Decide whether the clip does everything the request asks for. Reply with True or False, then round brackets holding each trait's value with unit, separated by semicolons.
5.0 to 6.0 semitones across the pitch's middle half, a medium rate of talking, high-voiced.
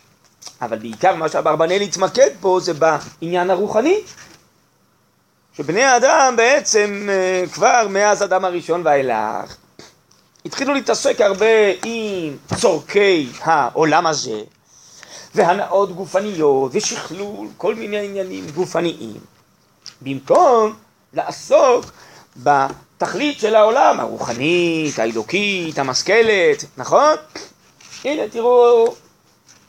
False (5.6 semitones; 85 wpm; 195 Hz)